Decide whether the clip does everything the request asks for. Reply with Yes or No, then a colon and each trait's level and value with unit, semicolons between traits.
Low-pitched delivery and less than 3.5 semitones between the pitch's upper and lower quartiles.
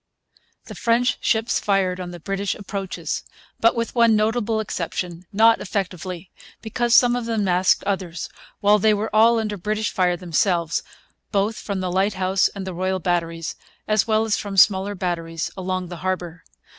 No: high, 195 Hz; average, 3.1 semitones